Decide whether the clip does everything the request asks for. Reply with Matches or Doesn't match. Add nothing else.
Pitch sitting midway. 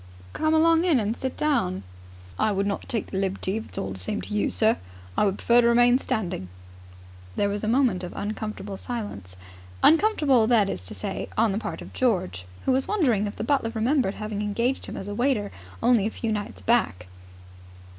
Doesn't match